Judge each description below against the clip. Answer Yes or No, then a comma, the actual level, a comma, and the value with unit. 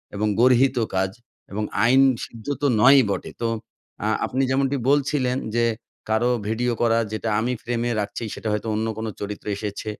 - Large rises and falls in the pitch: No, average, 3.0 semitones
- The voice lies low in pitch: Yes, low, 115 Hz